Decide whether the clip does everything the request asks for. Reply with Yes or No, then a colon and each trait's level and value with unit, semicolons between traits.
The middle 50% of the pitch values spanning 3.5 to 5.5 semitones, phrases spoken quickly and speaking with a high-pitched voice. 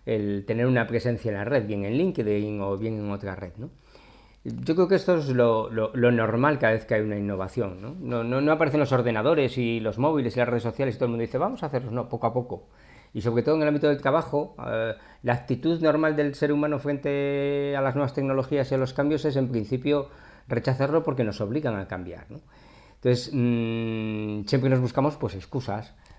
No: average, 4.2 semitones; fast, 225 wpm; low, 125 Hz